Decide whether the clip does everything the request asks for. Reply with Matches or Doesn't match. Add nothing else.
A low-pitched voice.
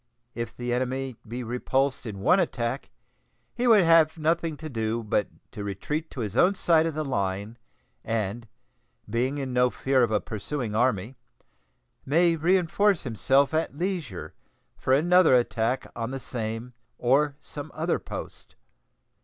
Matches